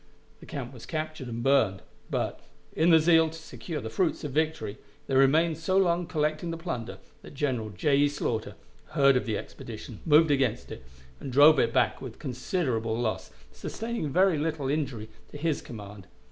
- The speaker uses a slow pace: No, average, 180 wpm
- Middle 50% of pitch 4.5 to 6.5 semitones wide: Yes, average, 4.9 semitones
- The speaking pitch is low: No, medium, 145 Hz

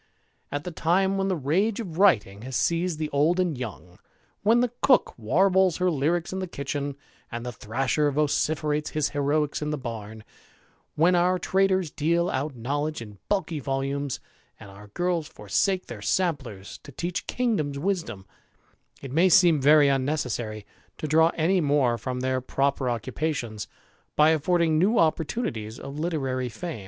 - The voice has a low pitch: No, medium, 150 Hz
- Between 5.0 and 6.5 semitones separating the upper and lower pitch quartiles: Yes, average, 5.3 semitones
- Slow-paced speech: No, average, 160 wpm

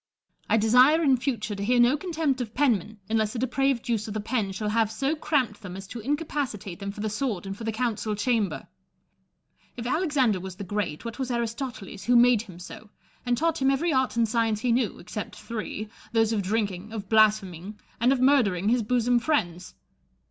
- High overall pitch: Yes, high, 225 Hz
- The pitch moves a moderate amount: Yes, average, 3.5 semitones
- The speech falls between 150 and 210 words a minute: Yes, fast, 205 wpm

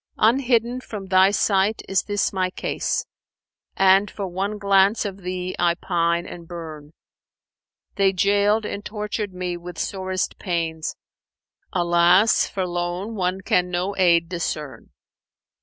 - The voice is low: No, medium, 185 Hz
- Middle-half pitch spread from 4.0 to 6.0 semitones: No, narrow, 2.5 semitones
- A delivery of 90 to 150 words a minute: Yes, average, 140 wpm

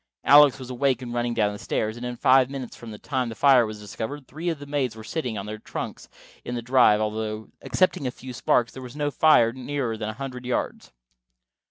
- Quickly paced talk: Yes, fast, 230 wpm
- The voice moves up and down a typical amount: Yes, average, 3.6 semitones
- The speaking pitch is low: Yes, low, 125 Hz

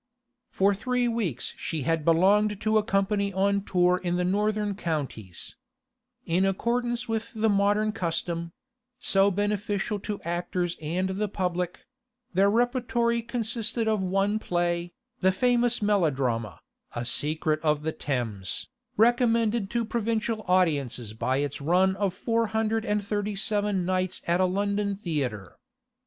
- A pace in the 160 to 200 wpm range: No, slow, 135 wpm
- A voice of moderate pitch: No, high, 200 Hz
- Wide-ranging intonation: No, average, 4.2 semitones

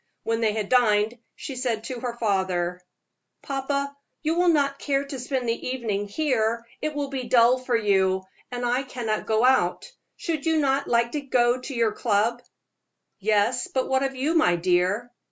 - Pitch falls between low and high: No, high, 245 Hz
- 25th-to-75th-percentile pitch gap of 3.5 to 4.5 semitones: Yes, average, 3.8 semitones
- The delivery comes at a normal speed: Yes, average, 180 wpm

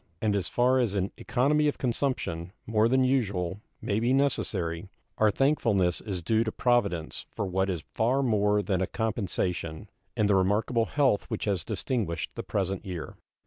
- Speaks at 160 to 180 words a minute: Yes, average, 170 wpm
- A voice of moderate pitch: No, low, 105 Hz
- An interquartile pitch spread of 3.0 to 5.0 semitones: Yes, average, 4.6 semitones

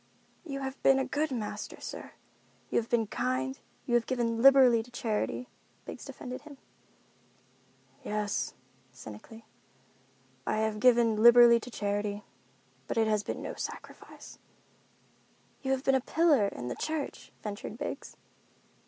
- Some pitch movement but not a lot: Yes, average, 4.0 semitones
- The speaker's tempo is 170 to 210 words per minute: No, average, 140 wpm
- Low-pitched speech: No, high, 235 Hz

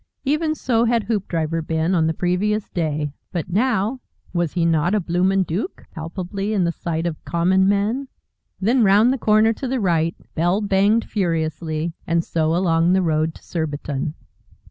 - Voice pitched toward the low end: No, medium, 180 Hz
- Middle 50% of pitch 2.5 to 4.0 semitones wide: No, average, 4.4 semitones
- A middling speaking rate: Yes, average, 165 wpm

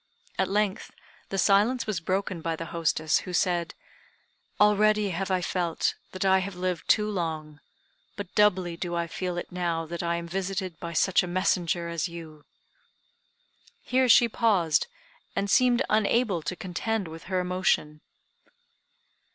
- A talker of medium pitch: Yes, medium, 180 Hz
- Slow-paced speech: No, average, 150 wpm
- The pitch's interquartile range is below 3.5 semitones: Yes, average, 2.9 semitones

